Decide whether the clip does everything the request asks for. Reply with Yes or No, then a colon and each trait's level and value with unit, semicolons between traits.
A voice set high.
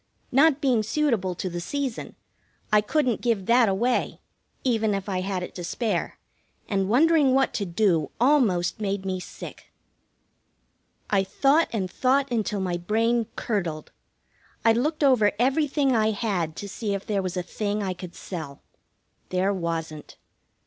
Yes: high, 210 Hz